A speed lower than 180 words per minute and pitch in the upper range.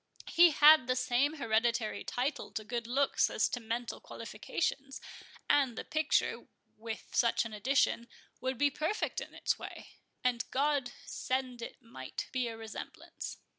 Yes: average, 145 wpm; very high, 250 Hz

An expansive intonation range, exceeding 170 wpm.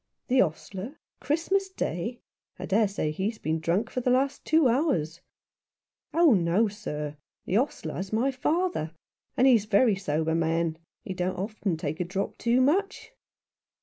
No: wide, 7.5 semitones; average, 165 wpm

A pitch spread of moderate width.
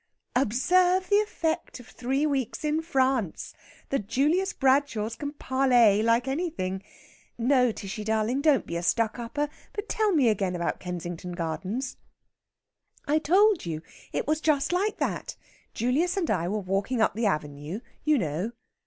No: wide, 7.0 semitones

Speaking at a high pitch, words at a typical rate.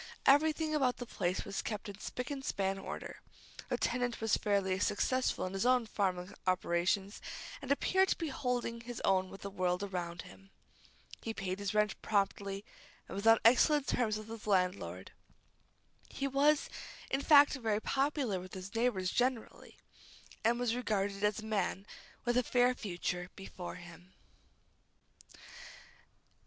Yes: high, 210 Hz; average, 150 wpm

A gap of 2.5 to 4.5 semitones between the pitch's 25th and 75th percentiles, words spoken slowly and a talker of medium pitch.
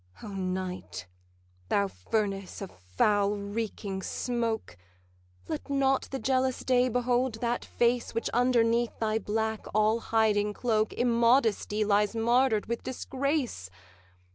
No: average, 3.1 semitones; slow, 115 wpm; high, 225 Hz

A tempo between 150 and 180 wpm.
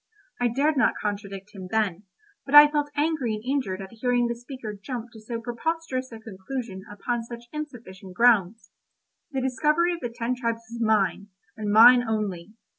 Yes: average, 175 wpm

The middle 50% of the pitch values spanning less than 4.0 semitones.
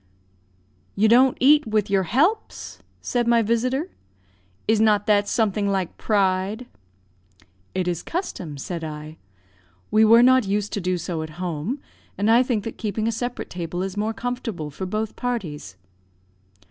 No: average, 4.4 semitones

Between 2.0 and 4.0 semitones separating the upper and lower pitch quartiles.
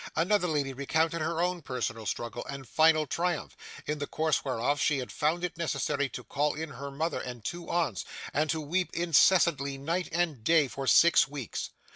Yes: average, 3.6 semitones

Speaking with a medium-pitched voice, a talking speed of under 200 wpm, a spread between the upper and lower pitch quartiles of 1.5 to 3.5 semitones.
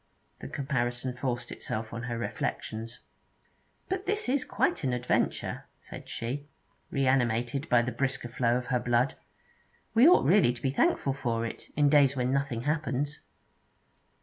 No: low, 130 Hz; average, 150 wpm; average, 2.9 semitones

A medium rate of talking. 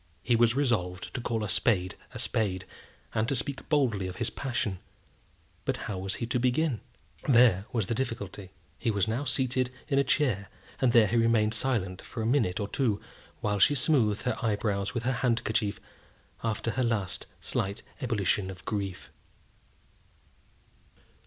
Yes: average, 165 wpm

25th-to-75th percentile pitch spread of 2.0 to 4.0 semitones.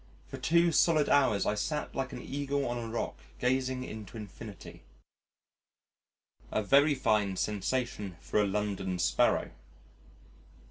No: average, 5.0 semitones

